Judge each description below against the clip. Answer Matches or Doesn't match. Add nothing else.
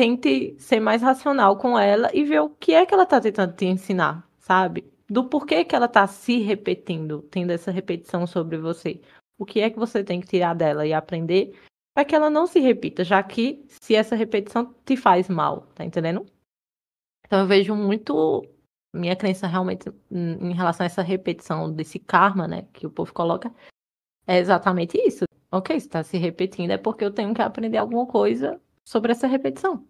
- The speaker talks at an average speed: Doesn't match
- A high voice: Matches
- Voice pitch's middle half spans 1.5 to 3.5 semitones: Doesn't match